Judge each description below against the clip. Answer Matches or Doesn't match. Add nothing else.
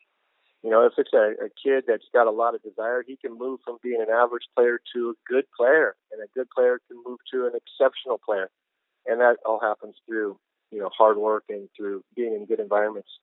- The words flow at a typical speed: Doesn't match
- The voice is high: Matches